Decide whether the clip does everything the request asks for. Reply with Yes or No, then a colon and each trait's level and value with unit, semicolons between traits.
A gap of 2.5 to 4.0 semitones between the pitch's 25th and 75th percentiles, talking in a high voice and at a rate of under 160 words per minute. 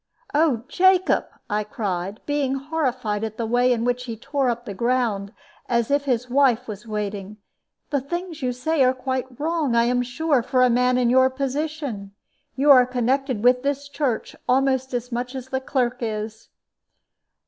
No: average, 2.9 semitones; very high, 250 Hz; average, 175 wpm